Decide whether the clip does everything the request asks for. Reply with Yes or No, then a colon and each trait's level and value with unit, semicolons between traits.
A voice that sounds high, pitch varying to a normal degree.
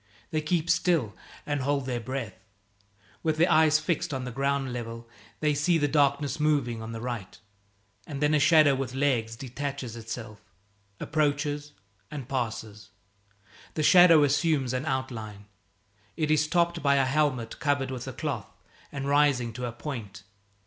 No: medium, 140 Hz; average, 3.8 semitones